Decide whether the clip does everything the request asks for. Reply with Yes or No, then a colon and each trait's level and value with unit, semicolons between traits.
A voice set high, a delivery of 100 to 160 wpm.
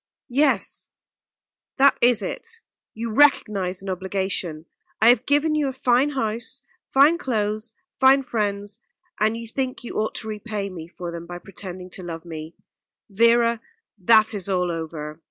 Yes: high, 215 Hz; average, 155 wpm